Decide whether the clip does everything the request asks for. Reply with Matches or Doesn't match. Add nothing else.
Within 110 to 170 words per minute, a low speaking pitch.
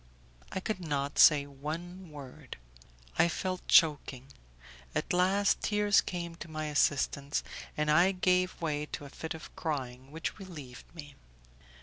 Doesn't match